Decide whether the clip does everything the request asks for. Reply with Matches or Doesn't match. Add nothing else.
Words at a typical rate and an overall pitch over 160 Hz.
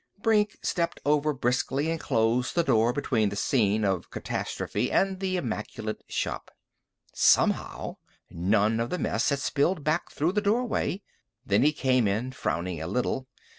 Doesn't match